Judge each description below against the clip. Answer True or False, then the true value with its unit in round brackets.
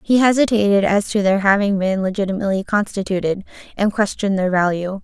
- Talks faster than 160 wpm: False (155 wpm)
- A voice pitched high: True (200 Hz)